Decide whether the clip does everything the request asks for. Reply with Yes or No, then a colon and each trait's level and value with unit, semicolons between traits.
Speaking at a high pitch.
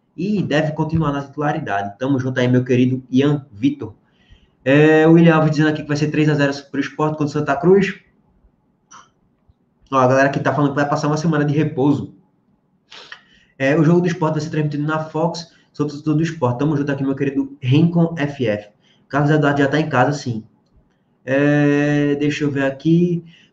No: medium, 145 Hz